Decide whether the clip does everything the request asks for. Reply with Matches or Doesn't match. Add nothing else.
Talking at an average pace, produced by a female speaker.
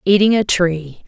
Matches